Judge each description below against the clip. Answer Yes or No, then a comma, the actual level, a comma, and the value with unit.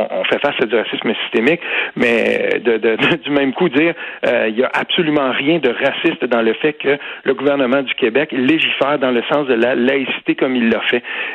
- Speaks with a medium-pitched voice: Yes, medium, 145 Hz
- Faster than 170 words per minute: Yes, fast, 220 wpm